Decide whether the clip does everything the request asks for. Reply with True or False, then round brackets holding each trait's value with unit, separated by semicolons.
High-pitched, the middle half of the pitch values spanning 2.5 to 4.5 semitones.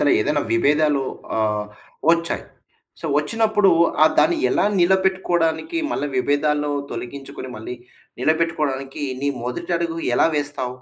False (150 Hz; 3.8 semitones)